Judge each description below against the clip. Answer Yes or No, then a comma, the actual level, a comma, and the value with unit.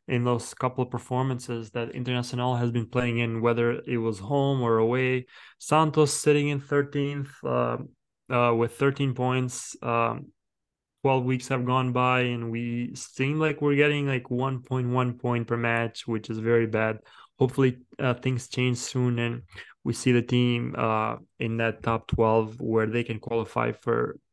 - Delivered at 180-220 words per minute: No, average, 165 wpm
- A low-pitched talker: Yes, low, 125 Hz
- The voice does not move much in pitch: Yes, narrow, 1.9 semitones